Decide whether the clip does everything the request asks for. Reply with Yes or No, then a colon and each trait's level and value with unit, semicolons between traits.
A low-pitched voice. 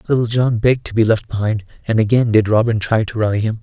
Yes: low, 110 Hz